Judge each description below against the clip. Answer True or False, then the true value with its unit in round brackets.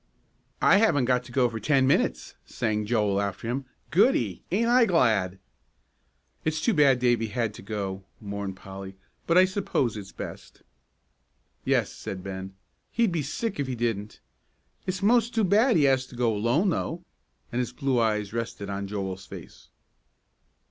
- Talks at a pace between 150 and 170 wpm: True (165 wpm)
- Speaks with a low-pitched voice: True (120 Hz)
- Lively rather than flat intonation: True (8.0 semitones)